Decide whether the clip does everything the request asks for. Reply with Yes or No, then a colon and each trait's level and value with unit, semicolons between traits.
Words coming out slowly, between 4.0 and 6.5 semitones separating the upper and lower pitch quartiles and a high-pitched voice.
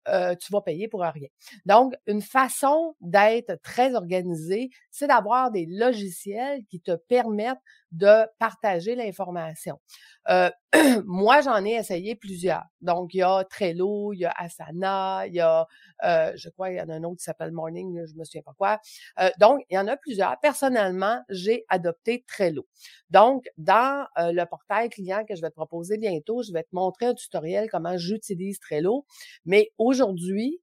No: average, 180 wpm; average, 5.0 semitones; high, 200 Hz